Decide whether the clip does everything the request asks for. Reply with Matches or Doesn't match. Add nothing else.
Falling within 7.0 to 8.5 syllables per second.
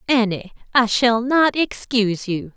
Doesn't match